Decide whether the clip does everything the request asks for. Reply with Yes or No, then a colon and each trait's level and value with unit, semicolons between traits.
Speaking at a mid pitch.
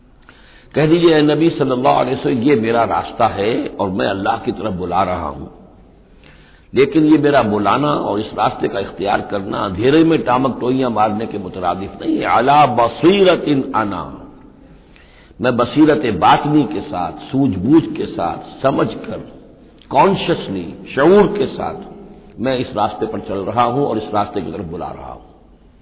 No: low, 130 Hz